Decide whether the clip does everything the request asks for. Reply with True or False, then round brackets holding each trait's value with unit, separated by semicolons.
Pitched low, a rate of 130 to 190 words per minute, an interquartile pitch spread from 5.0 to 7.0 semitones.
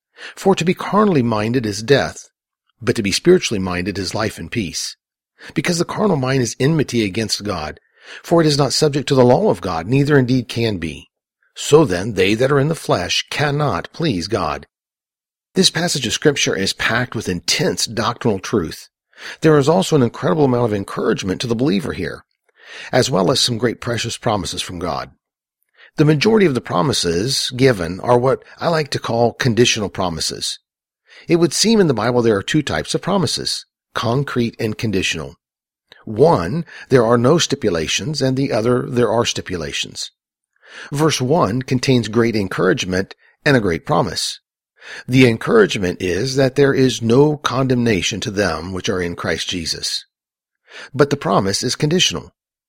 True (125 Hz; 170 wpm; 5.3 semitones)